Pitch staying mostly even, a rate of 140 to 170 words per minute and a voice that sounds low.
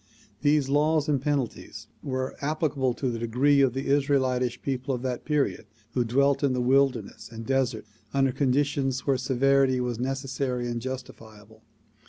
Yes: narrow, 2.0 semitones; average, 155 wpm; low, 130 Hz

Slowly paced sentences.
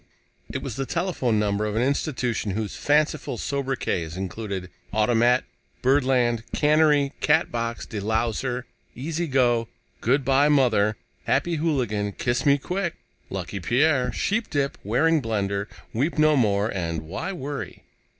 Yes: slow, 130 wpm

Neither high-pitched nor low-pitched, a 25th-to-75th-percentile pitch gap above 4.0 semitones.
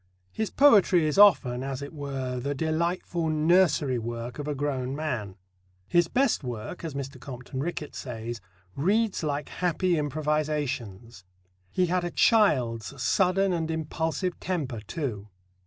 Yes: medium, 150 Hz; average, 5.3 semitones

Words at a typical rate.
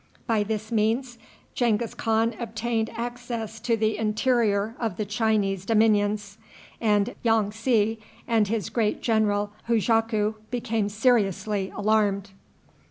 No: slow, 115 wpm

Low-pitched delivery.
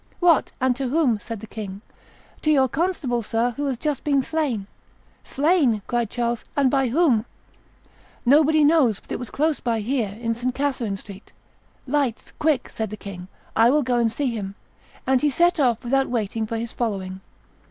No: high, 245 Hz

